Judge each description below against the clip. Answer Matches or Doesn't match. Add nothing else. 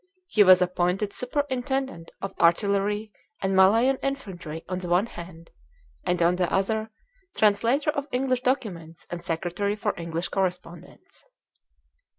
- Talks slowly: Matches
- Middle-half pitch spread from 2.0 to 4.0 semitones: Doesn't match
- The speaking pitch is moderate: Doesn't match